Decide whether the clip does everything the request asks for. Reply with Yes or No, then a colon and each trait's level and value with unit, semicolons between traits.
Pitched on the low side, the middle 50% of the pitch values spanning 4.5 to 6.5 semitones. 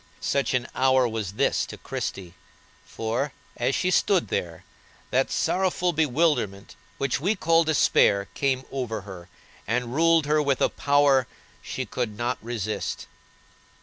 Yes: low, 130 Hz; average, 5.1 semitones